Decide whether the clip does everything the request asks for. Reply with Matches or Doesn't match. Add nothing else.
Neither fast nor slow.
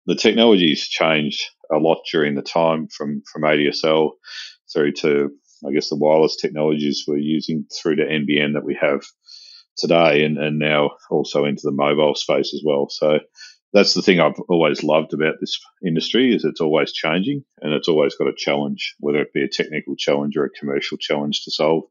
Matches